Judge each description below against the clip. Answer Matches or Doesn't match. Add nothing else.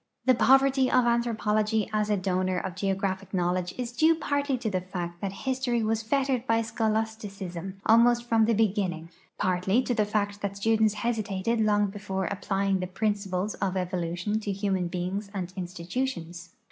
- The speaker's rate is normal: Matches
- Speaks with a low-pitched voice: Doesn't match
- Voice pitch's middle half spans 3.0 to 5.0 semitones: Matches